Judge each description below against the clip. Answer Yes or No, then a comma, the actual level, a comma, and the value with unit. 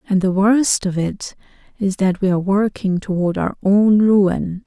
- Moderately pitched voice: No, high, 195 Hz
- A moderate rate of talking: Yes, average, 180 wpm